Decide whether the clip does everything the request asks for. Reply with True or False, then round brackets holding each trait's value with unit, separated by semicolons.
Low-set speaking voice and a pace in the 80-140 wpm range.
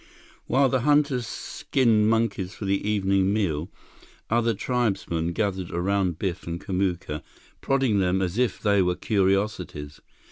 True (100 Hz; 135 wpm)